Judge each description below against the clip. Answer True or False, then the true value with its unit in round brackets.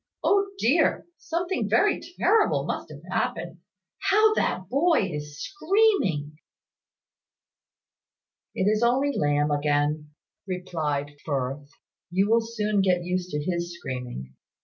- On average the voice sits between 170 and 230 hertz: True (185 Hz)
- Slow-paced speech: True (115 wpm)